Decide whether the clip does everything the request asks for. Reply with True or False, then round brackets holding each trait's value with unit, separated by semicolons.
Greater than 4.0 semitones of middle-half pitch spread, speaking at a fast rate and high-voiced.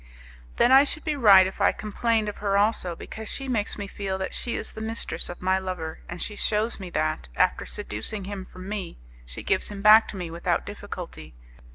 False (2.9 semitones; 215 wpm; 200 Hz)